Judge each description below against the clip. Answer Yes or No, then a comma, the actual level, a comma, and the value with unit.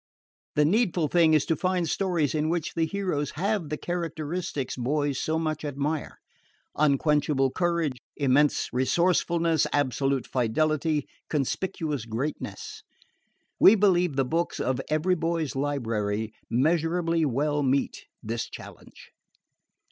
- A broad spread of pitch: No, average, 3.7 semitones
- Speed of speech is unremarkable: No, slow, 115 wpm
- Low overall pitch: No, medium, 155 Hz